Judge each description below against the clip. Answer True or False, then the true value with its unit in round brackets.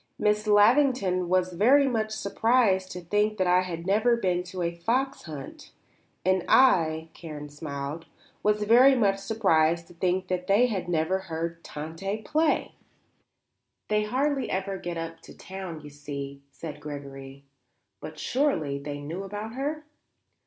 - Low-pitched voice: False (185 Hz)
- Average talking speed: True (150 wpm)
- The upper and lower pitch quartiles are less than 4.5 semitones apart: False (5.0 semitones)